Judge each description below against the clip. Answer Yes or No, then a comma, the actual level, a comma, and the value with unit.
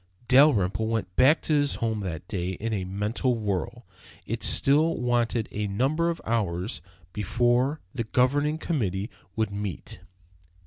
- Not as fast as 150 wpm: Yes, average, 140 wpm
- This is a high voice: No, low, 115 Hz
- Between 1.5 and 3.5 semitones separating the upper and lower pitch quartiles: No, average, 4.9 semitones